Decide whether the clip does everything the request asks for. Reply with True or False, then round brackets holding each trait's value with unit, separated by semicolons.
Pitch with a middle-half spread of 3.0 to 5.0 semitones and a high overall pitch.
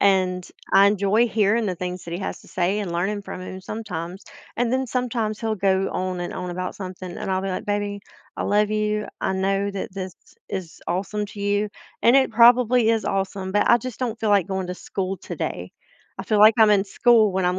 False (2.5 semitones; 200 Hz)